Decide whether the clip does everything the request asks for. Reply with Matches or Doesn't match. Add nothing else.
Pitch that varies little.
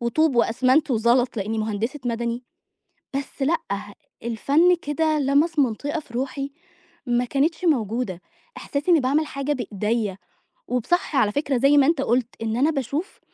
Doesn't match